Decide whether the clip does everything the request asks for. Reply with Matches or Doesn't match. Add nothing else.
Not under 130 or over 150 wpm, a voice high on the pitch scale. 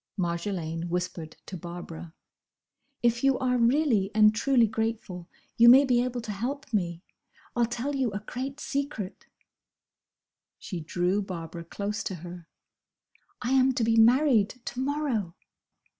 Matches